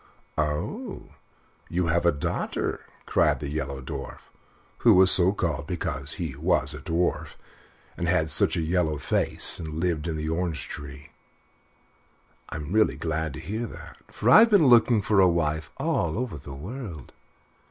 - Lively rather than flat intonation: No, average, 3.7 semitones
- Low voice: Yes, very low, 80 Hz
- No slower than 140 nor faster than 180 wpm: Yes, average, 160 wpm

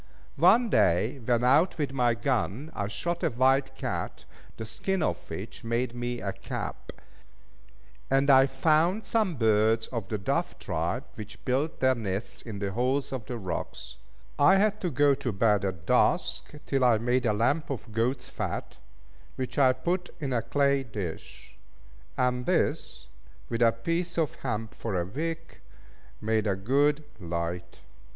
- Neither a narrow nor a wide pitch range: Yes, average, 4.8 semitones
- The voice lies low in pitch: Yes, low, 125 Hz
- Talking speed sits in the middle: Yes, average, 160 wpm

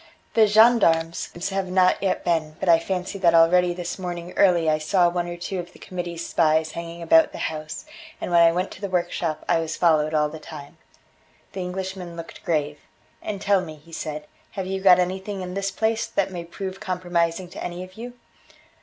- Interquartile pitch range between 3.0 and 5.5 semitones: No, narrow, 2.4 semitones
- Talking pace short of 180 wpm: No, fast, 205 wpm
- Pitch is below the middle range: No, medium, 175 Hz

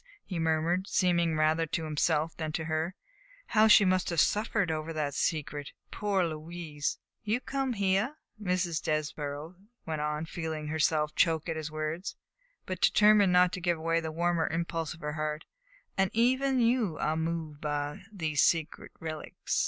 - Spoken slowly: No, average, 165 wpm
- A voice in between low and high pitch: Yes, medium, 165 Hz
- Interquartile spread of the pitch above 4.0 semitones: No, average, 3.0 semitones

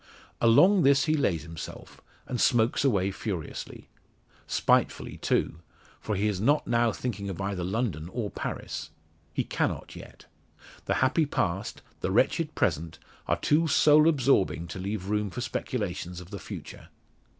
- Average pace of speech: Yes, average, 150 wpm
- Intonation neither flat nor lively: No, wide, 6.0 semitones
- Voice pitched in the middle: No, low, 105 Hz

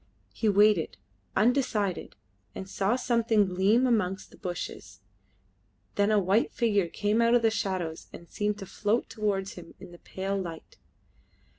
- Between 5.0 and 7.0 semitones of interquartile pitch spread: No, average, 2.9 semitones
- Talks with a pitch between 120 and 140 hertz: No, high, 205 Hz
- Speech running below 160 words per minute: Yes, average, 150 wpm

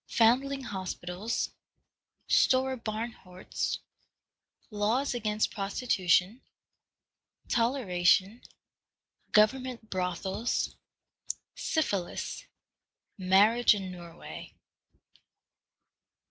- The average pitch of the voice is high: Yes, high, 215 Hz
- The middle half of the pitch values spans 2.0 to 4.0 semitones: No, average, 4.4 semitones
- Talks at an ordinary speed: No, slow, 50 wpm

